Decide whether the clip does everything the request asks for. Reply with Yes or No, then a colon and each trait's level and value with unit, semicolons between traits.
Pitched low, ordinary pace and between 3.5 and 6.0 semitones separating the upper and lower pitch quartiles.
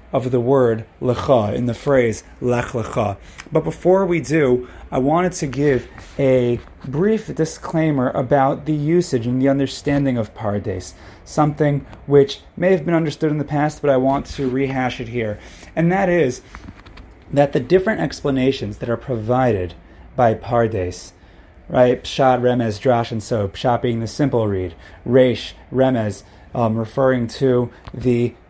Yes: low, 125 Hz; average, 155 wpm; average, 4.6 semitones